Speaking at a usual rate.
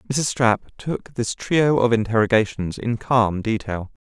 Yes: average, 145 wpm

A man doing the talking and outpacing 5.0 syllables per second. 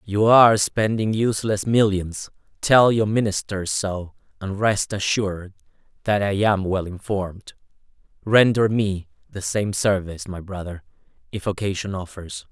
No: male; 4.5 syllables/s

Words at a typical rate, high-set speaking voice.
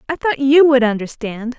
Yes: average, 190 wpm; very high, 260 Hz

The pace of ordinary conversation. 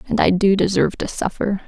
No: fast, 215 wpm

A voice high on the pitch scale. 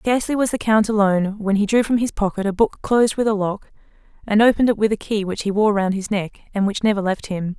Yes: high, 210 Hz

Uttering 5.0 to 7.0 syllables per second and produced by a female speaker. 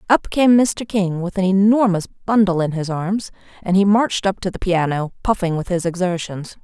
Yes: 5.2 syllables/s; female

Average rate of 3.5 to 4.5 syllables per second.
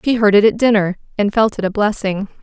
No: 5.9 syllables/s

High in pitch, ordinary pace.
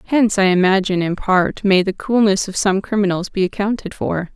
Yes: high, 195 Hz; average, 195 wpm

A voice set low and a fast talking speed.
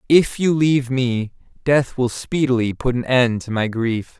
No: low, 125 Hz; average, 185 wpm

